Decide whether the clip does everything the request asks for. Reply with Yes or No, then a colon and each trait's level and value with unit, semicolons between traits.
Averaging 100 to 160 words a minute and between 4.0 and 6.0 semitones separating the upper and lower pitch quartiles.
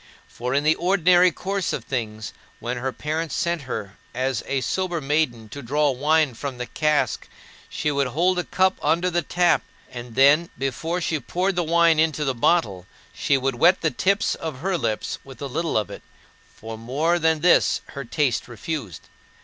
No: average, 185 wpm; average, 5.2 semitones